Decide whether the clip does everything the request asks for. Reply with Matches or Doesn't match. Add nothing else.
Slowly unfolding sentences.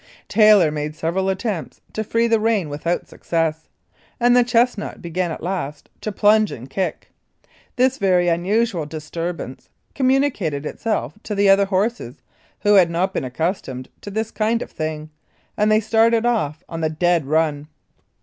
Doesn't match